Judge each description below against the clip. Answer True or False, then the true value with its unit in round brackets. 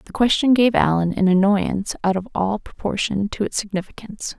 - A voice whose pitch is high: True (200 Hz)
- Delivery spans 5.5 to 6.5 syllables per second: True (5.6 syllables/s)